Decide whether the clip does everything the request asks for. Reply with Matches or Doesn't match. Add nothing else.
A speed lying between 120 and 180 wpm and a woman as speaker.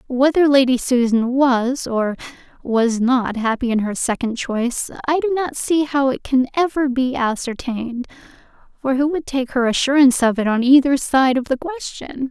Matches